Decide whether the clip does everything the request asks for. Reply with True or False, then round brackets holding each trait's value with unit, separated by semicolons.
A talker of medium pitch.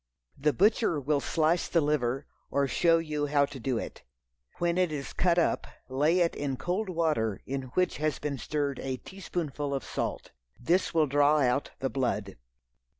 True (150 Hz)